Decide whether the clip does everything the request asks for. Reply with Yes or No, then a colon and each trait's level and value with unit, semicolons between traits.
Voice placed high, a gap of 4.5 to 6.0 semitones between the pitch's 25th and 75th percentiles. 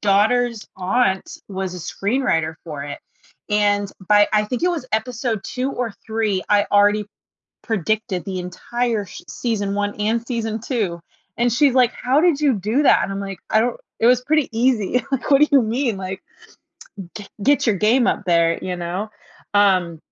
No: high, 215 Hz; average, 4.0 semitones